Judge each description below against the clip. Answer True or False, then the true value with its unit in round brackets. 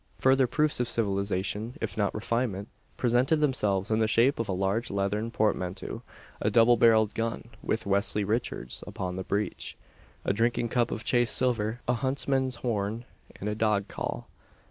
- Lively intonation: False (3.2 semitones)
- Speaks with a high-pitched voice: False (110 Hz)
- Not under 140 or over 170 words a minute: True (165 wpm)